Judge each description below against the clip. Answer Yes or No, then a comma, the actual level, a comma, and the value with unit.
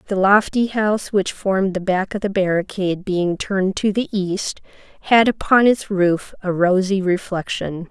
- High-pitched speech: Yes, high, 195 Hz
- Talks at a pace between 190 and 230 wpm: No, average, 165 wpm